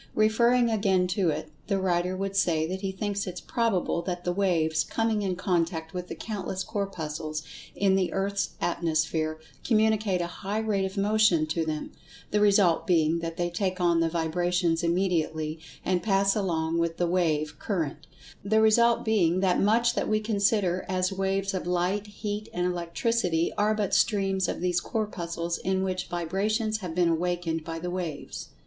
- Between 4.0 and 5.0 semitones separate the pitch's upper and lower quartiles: No, average, 3.1 semitones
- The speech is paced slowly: No, average, 170 wpm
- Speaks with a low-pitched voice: No, medium, 185 Hz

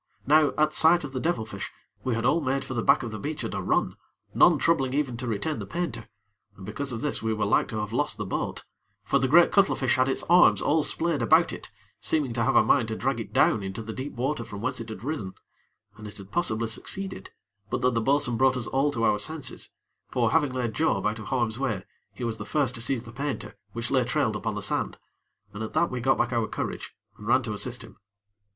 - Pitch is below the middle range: Yes, low, 125 Hz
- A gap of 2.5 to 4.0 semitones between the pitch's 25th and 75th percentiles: No, average, 4.6 semitones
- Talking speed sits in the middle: No, fast, 250 wpm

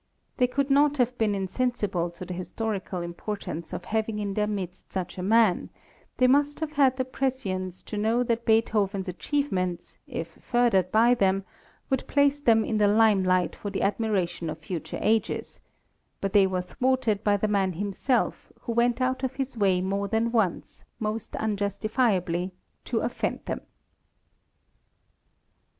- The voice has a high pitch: Yes, high, 210 Hz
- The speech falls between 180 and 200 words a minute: No, average, 160 wpm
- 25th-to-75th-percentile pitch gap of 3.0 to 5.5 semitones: Yes, average, 4.5 semitones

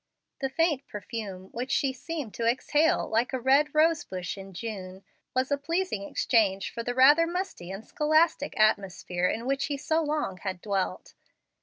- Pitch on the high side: Yes, very high, 250 Hz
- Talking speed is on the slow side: No, average, 165 wpm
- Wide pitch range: Yes, wide, 7.2 semitones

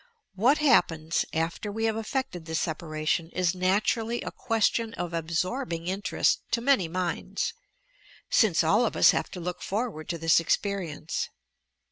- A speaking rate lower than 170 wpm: Yes, average, 155 wpm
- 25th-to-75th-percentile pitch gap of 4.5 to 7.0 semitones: Yes, average, 5.3 semitones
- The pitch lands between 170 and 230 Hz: Yes, medium, 185 Hz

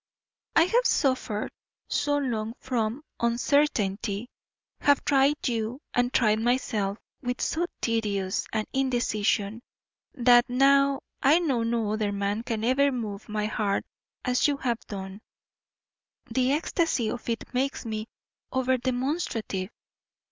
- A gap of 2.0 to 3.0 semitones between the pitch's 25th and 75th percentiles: No, average, 3.9 semitones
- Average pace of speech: No, slow, 125 wpm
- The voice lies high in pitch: Yes, high, 240 Hz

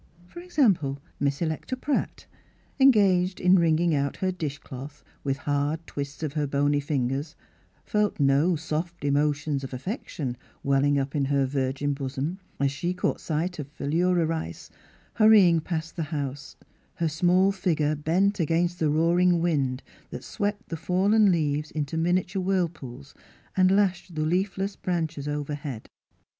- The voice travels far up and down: No, average, 4.1 semitones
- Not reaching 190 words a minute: Yes, average, 150 wpm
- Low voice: No, medium, 160 Hz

